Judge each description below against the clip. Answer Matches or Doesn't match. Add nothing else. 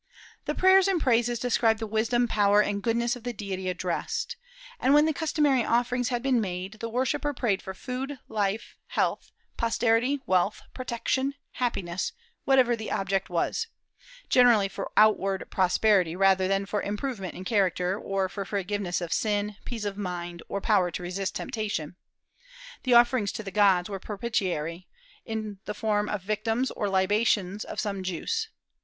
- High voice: Matches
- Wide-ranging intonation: Doesn't match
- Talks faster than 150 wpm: Matches